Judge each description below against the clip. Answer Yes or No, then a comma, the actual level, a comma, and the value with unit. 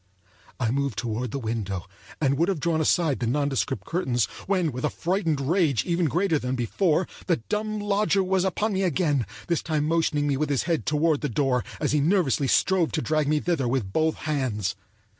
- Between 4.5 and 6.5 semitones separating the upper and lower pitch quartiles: Yes, average, 4.9 semitones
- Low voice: No, medium, 150 Hz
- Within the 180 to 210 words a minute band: Yes, average, 195 wpm